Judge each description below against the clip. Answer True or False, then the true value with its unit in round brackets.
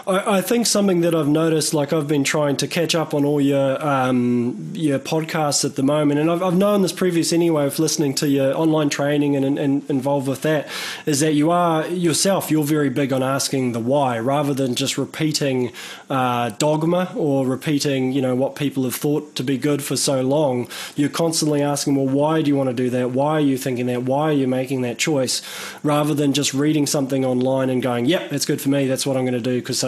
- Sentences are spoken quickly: True (230 wpm)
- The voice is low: False (145 Hz)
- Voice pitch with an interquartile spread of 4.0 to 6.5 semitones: False (2.5 semitones)